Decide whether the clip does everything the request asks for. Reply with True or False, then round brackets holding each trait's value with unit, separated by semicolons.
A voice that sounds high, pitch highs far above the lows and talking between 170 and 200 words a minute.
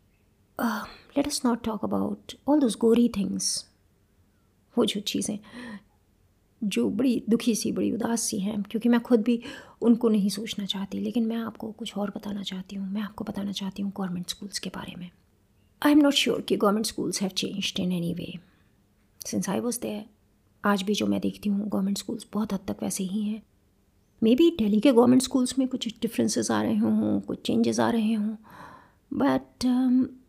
False (205 Hz; 4.6 semitones; 180 wpm)